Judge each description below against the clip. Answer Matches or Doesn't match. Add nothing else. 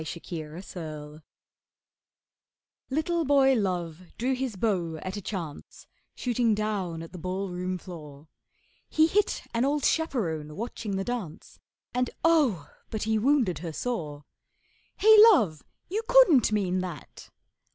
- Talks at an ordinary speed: Doesn't match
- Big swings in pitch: Matches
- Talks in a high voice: Matches